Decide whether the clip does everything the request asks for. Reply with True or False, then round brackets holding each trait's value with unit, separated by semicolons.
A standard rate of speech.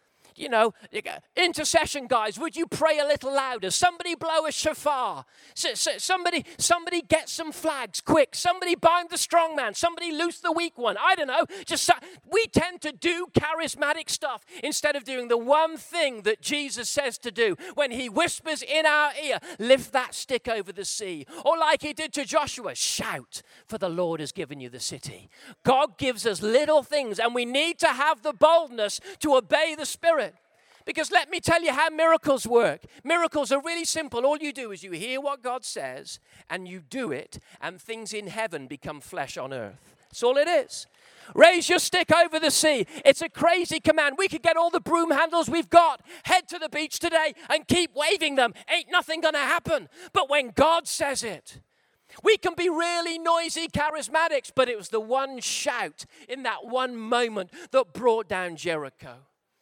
True (190 wpm)